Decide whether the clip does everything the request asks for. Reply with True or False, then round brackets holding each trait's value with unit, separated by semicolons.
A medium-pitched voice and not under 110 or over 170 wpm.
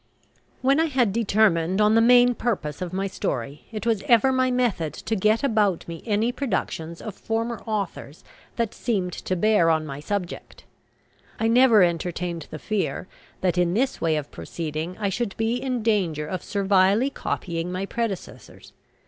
False (200 Hz; 165 wpm)